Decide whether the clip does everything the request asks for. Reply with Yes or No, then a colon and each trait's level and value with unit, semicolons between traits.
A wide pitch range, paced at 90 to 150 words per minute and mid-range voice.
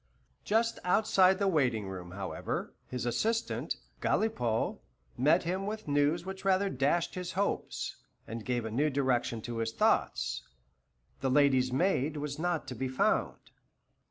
Yes: wide, 7.5 semitones; average, 145 wpm; medium, 145 Hz